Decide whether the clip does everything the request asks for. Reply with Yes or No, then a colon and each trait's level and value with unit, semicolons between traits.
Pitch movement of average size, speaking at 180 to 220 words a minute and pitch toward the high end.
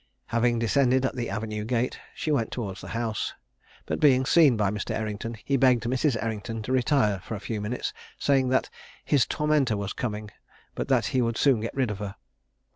No: average, 3.5 semitones; average, 200 wpm; low, 115 Hz